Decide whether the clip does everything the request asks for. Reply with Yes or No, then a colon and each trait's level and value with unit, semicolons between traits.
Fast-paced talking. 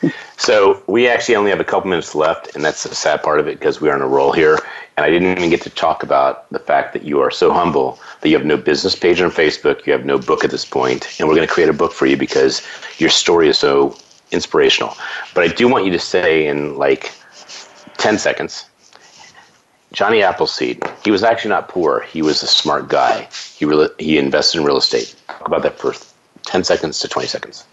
Yes: fast, 230 wpm